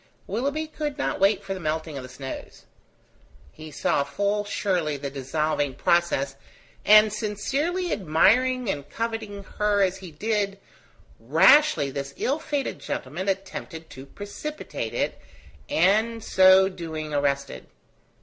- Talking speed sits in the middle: No, slow, 130 wpm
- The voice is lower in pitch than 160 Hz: No, high, 190 Hz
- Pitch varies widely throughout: Yes, wide, 6.2 semitones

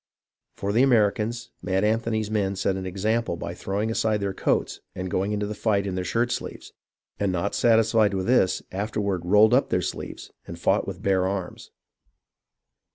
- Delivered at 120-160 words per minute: No, average, 175 wpm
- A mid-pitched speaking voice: No, low, 100 Hz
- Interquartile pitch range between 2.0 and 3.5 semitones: Yes, average, 2.8 semitones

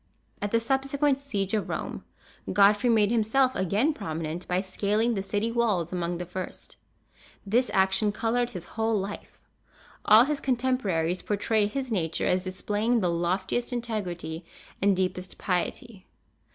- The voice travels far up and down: No, average, 4.2 semitones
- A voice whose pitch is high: Yes, high, 205 Hz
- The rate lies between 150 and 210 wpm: No, average, 140 wpm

